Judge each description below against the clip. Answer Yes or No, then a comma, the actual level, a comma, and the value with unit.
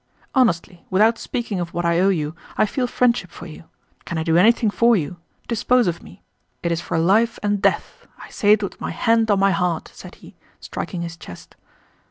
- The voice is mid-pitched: No, high, 195 Hz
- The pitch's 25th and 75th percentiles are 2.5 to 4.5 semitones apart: No, average, 5.0 semitones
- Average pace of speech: No, fast, 210 wpm